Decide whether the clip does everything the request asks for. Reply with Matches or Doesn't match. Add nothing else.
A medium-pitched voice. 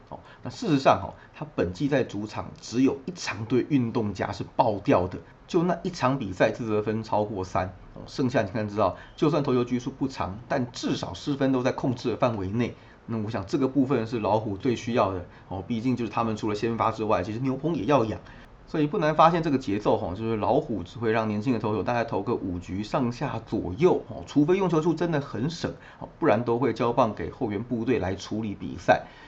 Doesn't match